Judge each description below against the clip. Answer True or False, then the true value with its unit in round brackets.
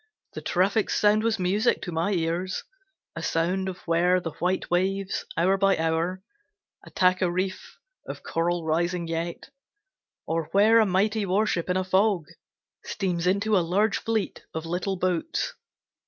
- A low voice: False (185 Hz)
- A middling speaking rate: True (155 wpm)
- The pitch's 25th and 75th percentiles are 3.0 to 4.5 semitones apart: False (2.5 semitones)